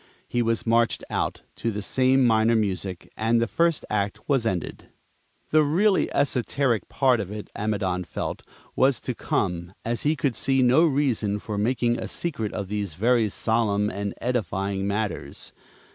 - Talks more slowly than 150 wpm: No, average, 160 wpm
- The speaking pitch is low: Yes, low, 115 Hz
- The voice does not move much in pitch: No, average, 4.0 semitones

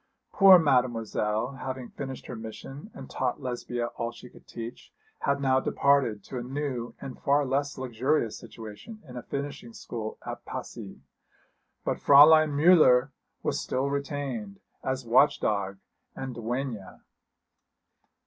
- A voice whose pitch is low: Yes, low, 130 Hz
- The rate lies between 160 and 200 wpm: No, slow, 135 wpm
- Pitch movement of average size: Yes, average, 3.1 semitones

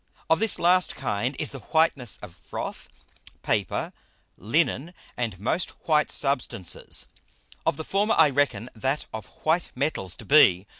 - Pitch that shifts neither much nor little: No, wide, 6.4 semitones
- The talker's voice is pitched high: No, medium, 140 Hz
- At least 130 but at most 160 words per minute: Yes, average, 145 wpm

